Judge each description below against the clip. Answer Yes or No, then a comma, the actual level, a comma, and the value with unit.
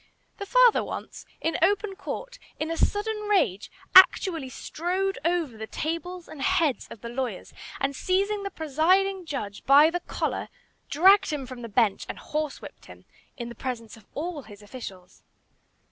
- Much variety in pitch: Yes, wide, 7.0 semitones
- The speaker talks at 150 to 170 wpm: Yes, average, 160 wpm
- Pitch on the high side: Yes, very high, 320 Hz